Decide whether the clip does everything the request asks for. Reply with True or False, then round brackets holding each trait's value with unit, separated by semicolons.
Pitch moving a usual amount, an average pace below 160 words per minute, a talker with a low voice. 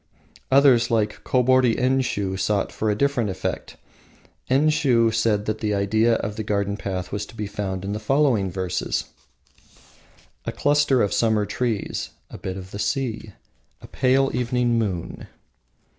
True (3.9 semitones; 145 wpm; 110 Hz)